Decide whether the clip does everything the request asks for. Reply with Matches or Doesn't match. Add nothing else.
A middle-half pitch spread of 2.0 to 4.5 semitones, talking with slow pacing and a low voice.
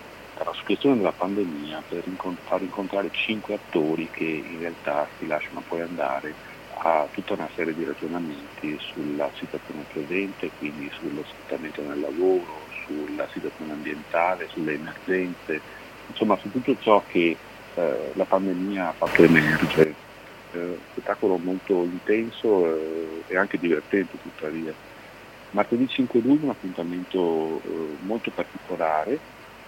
Doesn't match